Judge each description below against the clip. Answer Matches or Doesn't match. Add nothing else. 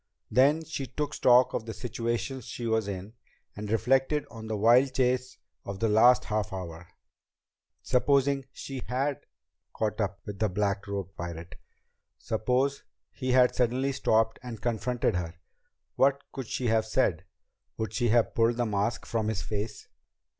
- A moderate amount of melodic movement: Matches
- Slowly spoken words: Doesn't match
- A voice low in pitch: Matches